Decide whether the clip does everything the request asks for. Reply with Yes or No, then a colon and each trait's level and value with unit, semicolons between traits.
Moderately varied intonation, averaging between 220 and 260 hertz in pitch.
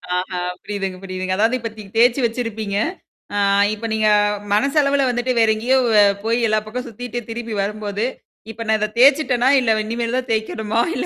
No: narrow, 2.3 semitones; high, 225 Hz